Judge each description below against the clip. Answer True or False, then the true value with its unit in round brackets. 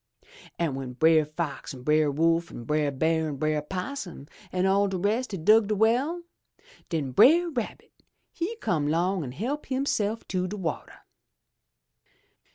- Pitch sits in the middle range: True (175 Hz)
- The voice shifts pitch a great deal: True (6.3 semitones)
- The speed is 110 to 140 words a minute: False (160 wpm)